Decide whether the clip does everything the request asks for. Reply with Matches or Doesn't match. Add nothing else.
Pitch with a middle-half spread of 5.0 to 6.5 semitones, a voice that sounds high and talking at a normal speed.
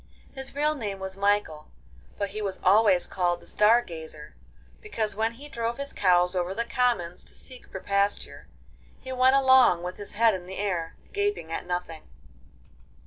Matches